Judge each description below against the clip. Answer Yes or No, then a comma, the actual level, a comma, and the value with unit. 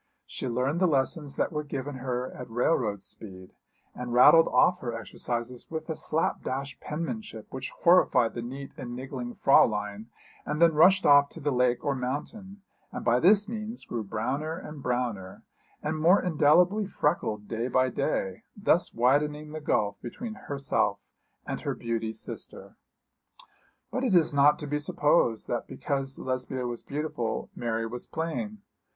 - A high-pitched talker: No, low, 135 Hz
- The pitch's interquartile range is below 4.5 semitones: No, average, 4.8 semitones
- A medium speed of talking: Yes, average, 160 wpm